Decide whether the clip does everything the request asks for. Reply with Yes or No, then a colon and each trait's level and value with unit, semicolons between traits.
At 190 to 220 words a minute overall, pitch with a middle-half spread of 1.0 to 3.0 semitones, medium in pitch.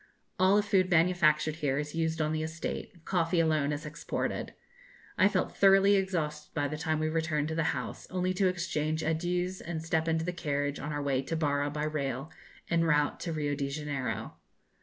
Yes: average, 195 wpm; narrow, 2.6 semitones; medium, 160 Hz